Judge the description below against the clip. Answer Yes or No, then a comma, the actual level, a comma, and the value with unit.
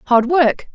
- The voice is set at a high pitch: Yes, very high, 270 Hz